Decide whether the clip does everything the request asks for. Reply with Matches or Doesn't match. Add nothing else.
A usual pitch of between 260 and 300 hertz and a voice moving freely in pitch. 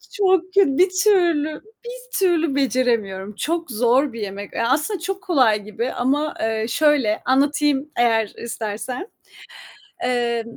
Matches